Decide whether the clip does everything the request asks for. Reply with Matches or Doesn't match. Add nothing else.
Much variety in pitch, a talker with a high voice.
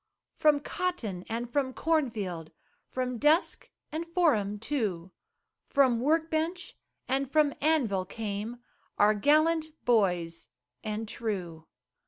Matches